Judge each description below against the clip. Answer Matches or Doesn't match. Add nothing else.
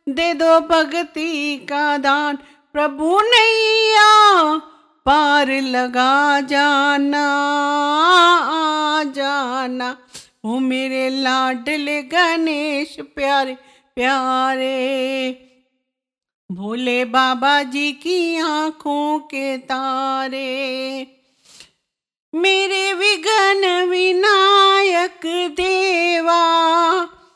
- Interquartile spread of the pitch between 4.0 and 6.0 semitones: Matches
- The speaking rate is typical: Doesn't match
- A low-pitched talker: Doesn't match